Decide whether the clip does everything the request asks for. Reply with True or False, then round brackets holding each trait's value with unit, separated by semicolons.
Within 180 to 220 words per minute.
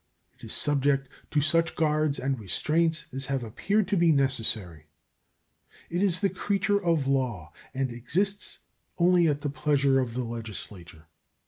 False (150 wpm)